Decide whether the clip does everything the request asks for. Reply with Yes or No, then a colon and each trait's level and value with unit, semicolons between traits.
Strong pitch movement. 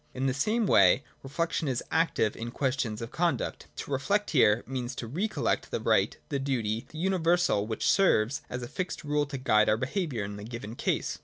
Yes: wide, 6.1 semitones